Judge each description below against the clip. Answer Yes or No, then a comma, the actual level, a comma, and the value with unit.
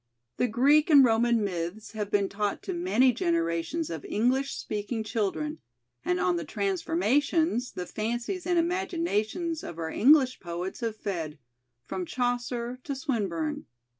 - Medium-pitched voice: No, high, 225 Hz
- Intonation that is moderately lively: No, wide, 6.6 semitones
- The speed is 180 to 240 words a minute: No, average, 140 wpm